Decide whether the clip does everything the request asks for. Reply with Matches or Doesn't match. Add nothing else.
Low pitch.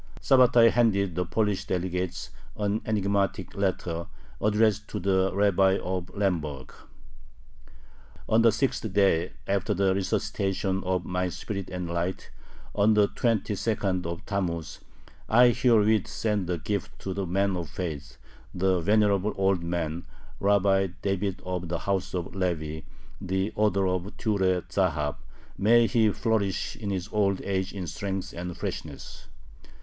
Matches